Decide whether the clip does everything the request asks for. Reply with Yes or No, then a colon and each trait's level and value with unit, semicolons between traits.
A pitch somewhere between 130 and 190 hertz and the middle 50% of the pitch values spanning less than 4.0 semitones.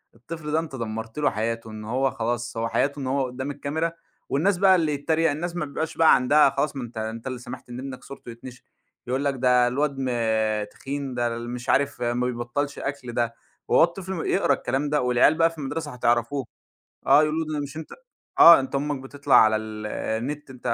Yes: low, 135 Hz; average, 3.6 semitones